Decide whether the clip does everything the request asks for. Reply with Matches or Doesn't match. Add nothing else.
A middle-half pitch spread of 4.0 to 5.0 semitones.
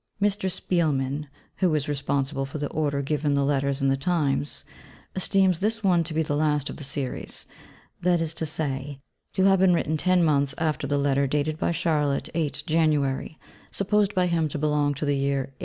Doesn't match